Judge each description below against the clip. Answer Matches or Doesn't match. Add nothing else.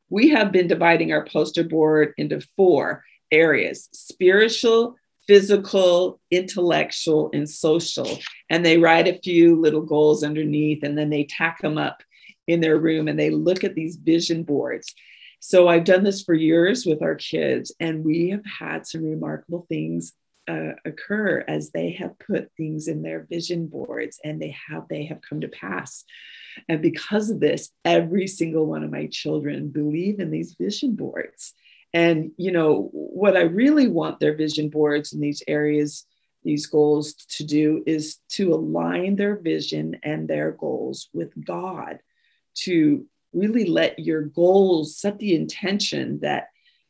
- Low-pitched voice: Doesn't match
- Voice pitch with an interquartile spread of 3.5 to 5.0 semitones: Matches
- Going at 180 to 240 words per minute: Doesn't match